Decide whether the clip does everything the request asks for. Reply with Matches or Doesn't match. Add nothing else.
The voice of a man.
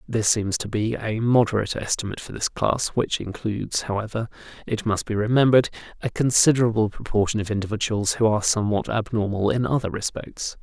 Matches